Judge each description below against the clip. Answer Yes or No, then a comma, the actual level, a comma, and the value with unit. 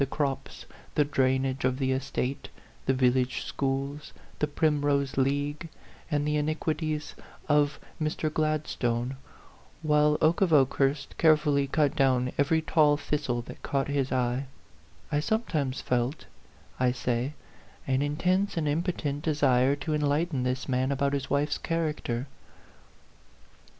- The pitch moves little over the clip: Yes, narrow, 2.3 semitones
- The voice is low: No, medium, 145 Hz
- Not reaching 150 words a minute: Yes, average, 140 wpm